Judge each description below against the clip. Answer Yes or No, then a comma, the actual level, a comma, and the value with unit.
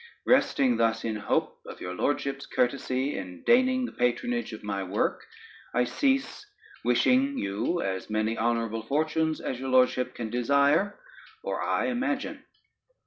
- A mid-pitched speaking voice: No, low, 130 Hz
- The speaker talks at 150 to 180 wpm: No, average, 140 wpm